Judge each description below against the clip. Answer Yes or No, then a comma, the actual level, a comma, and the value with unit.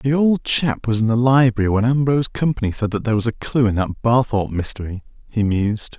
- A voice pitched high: No, low, 115 Hz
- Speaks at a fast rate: Yes, fast, 220 wpm